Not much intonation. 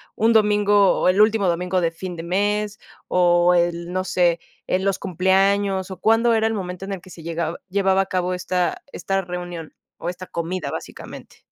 Yes: narrow, 2.2 semitones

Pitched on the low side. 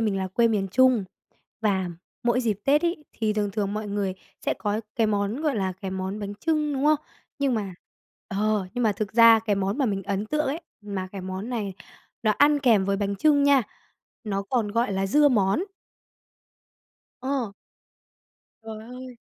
No: high, 215 Hz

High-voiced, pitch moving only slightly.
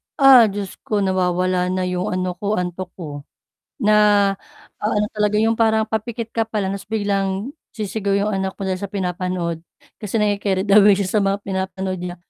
Yes: high, 200 Hz; narrow, 2.2 semitones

